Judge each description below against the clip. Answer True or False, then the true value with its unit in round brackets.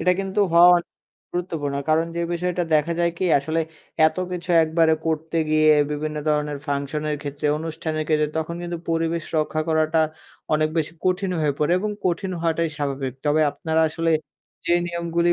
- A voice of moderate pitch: True (160 Hz)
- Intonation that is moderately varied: False (1.9 semitones)